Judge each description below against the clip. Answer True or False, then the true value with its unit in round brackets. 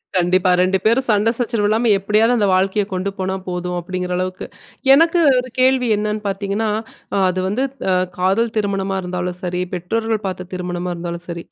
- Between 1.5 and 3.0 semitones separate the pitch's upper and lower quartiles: False (3.4 semitones)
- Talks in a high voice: True (195 Hz)